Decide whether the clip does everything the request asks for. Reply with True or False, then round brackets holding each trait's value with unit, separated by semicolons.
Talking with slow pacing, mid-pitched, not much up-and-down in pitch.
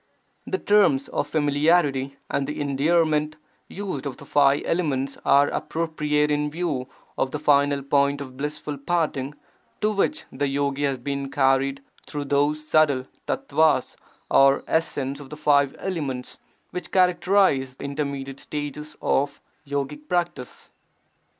True (130 wpm; 145 Hz; 2.1 semitones)